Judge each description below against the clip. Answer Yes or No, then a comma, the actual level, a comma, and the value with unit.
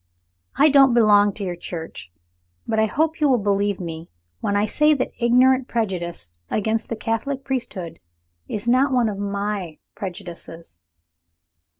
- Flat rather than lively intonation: No, wide, 5.4 semitones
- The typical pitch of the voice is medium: No, high, 210 Hz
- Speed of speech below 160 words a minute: Yes, average, 150 wpm